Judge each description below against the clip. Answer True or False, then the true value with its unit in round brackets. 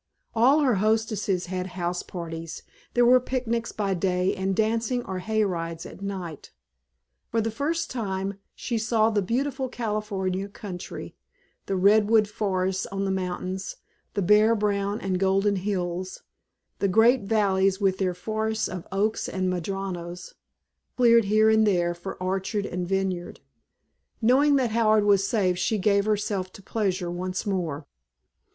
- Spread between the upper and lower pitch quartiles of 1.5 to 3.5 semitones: True (2.9 semitones)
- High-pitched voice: True (200 Hz)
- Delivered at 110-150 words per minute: True (145 wpm)